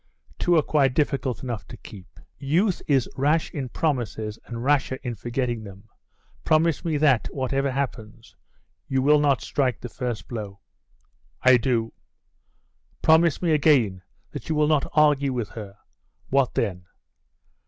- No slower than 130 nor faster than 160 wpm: Yes, average, 145 wpm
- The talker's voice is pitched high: No, low, 130 Hz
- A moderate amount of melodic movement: Yes, average, 4.4 semitones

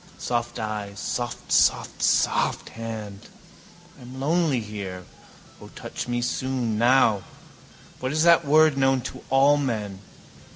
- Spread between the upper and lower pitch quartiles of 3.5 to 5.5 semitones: Yes, average, 3.9 semitones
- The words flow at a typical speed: No, slow, 130 wpm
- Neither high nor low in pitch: No, low, 120 Hz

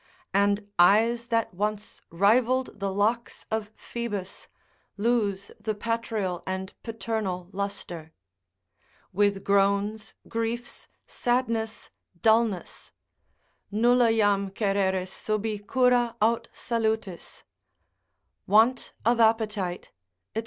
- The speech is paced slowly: Yes, slow, 90 wpm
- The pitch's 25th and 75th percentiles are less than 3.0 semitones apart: Yes, narrow, 2.5 semitones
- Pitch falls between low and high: No, high, 215 Hz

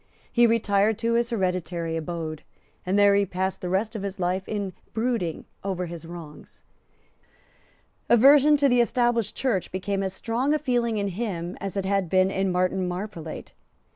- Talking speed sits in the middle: Yes, average, 170 wpm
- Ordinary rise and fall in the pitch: Yes, average, 4.2 semitones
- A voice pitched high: Yes, high, 195 Hz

